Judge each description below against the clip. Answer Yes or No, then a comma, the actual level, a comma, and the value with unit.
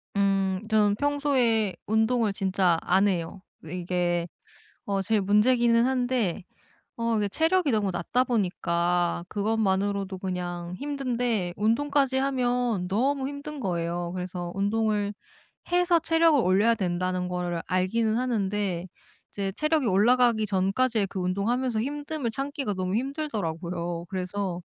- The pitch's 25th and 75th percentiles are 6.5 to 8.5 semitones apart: No, average, 5.3 semitones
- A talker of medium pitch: No, high, 205 Hz